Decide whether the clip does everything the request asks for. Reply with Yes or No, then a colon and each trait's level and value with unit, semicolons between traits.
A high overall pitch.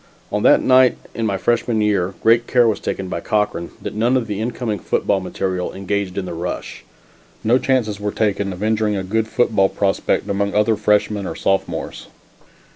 No: low, 105 Hz